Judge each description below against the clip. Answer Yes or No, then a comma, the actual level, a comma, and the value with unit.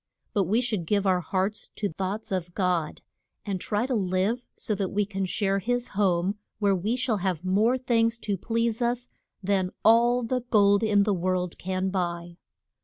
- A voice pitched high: Yes, high, 200 Hz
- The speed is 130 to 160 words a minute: No, average, 180 wpm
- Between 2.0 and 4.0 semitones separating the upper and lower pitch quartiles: Yes, average, 3.5 semitones